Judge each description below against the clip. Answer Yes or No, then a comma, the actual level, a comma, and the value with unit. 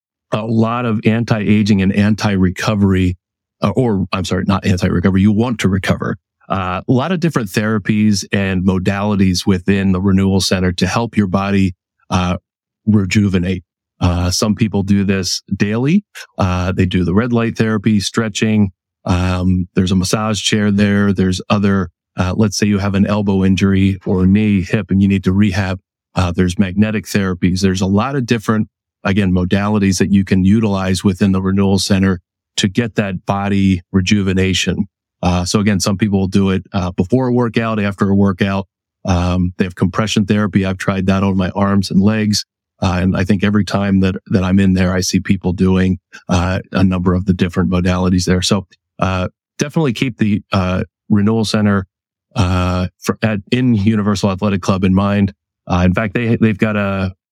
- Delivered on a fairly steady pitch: Yes, narrow, 2.1 semitones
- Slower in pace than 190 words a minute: Yes, average, 180 wpm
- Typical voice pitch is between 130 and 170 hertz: No, low, 100 Hz